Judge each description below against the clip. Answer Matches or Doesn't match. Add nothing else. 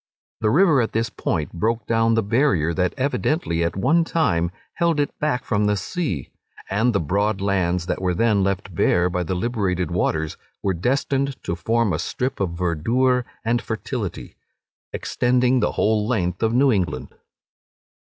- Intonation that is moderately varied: Doesn't match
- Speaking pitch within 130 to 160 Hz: Doesn't match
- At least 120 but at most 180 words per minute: Matches